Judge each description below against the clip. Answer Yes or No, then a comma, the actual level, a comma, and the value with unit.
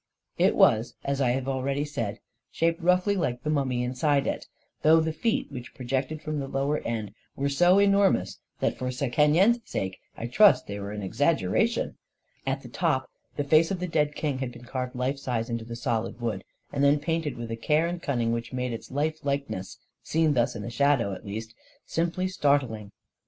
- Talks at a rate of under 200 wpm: No, fast, 205 wpm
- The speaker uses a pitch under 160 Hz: Yes, low, 135 Hz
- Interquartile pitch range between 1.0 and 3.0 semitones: No, average, 4.6 semitones